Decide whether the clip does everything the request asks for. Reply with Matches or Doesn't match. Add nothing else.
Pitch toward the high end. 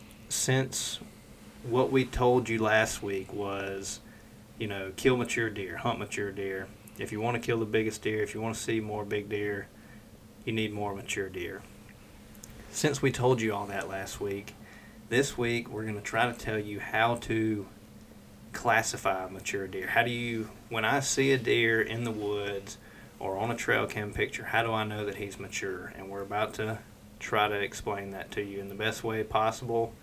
Doesn't match